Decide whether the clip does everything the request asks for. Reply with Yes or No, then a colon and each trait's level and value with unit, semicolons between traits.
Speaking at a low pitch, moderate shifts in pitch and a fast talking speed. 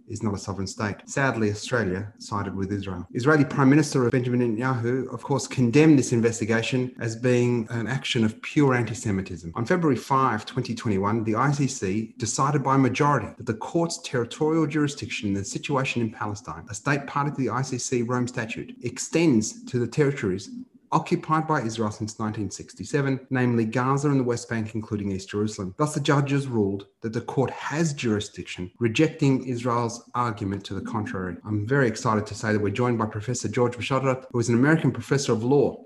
No: low, 120 Hz; average, 4.0 semitones; average, 180 wpm